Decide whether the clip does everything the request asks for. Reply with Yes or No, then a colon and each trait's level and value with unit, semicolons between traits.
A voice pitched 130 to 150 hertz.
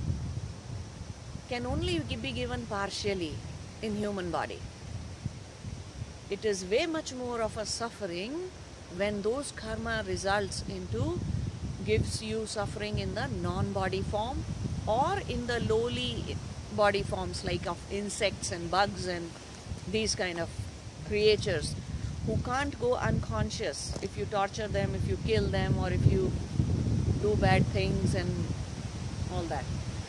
No: medium, 175 Hz